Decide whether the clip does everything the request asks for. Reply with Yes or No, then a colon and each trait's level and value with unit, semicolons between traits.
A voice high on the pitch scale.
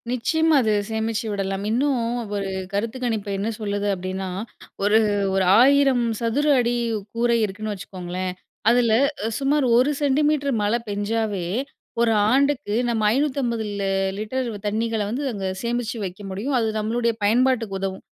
Yes: high, 225 Hz